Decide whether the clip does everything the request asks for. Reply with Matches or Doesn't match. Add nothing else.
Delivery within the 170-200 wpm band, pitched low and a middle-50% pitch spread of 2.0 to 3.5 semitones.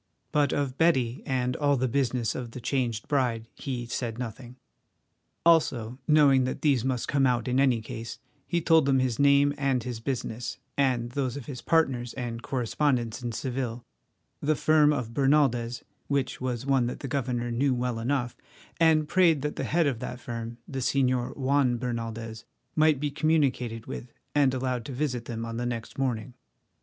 Matches